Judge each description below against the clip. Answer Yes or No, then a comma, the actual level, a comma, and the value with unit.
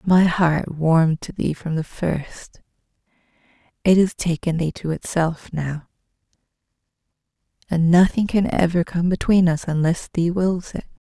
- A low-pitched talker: No, medium, 170 Hz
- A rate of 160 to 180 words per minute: No, average, 140 wpm